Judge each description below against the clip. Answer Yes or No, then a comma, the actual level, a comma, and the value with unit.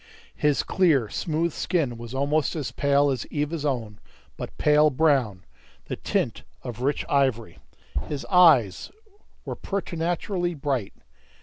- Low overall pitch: No, medium, 145 Hz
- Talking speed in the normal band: No, slow, 125 wpm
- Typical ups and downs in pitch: Yes, average, 4.1 semitones